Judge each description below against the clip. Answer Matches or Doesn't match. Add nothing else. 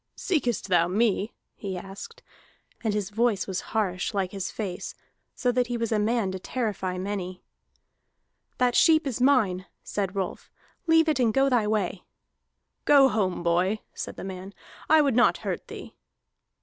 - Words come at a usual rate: Matches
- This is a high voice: Matches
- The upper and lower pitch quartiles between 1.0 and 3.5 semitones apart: Doesn't match